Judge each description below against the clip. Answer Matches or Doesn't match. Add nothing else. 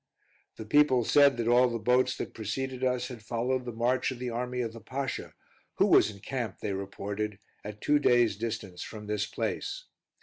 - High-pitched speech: Doesn't match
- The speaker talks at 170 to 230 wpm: Matches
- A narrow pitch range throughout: Doesn't match